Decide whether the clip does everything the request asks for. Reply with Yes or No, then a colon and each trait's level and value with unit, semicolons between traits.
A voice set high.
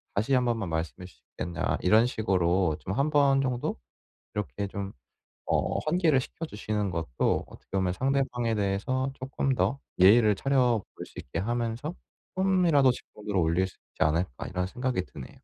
No: low, 110 Hz